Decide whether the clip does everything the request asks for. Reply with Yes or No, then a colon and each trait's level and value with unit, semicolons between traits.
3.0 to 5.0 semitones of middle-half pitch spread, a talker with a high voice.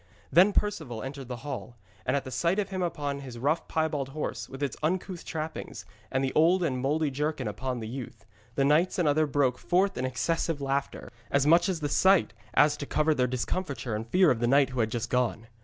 No: average, 3.9 semitones; medium, 140 Hz